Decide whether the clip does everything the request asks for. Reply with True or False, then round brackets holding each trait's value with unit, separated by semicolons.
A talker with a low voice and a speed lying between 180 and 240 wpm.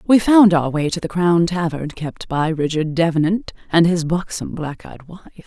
False (170 Hz; 200 wpm)